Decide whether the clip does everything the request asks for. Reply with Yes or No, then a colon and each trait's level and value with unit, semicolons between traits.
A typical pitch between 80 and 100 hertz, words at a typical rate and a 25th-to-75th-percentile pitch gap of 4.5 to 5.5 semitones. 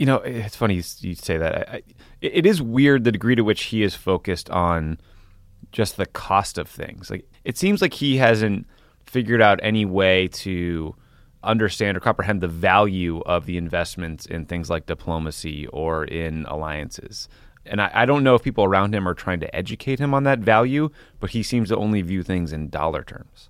Yes: very low, 95 Hz; average, 195 wpm; average, 5.0 semitones